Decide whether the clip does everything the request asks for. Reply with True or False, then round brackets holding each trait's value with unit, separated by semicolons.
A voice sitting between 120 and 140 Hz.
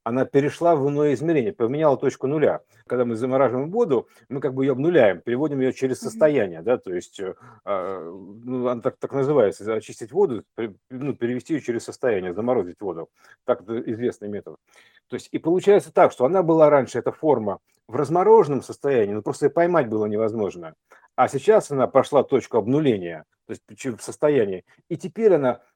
True (135 Hz)